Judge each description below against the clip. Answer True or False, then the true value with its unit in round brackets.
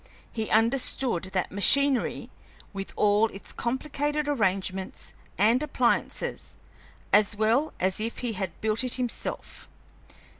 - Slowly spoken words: True (115 wpm)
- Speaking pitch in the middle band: False (225 Hz)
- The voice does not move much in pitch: False (4.4 semitones)